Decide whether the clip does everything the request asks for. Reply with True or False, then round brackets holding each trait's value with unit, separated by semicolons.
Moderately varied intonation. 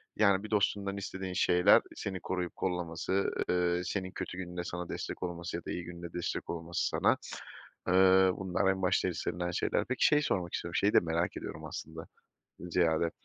False (1.7 semitones)